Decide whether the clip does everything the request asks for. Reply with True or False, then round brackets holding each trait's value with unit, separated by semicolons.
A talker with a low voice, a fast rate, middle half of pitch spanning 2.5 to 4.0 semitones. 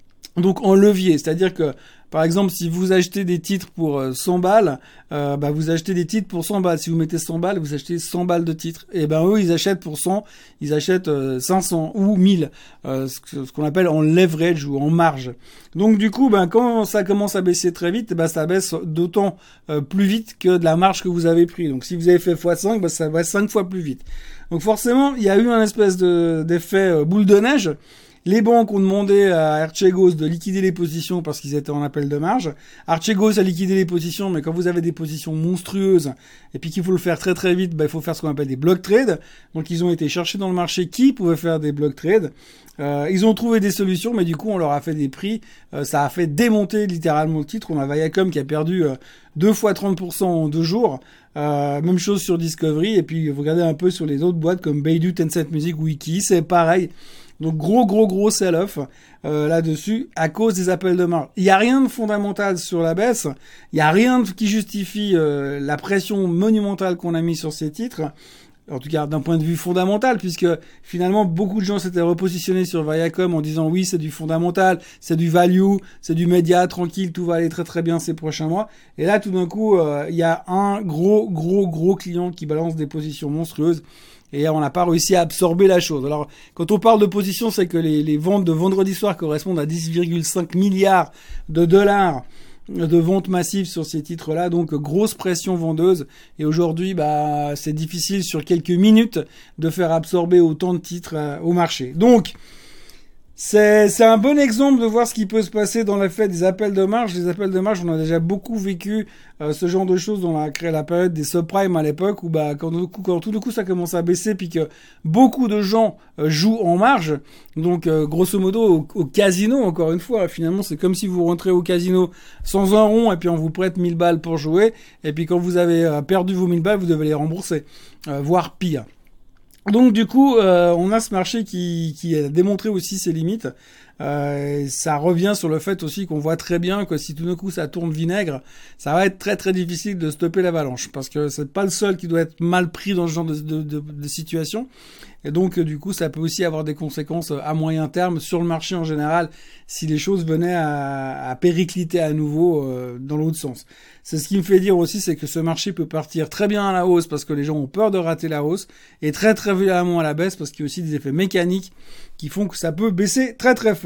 False (175 Hz; 235 wpm; 3.5 semitones)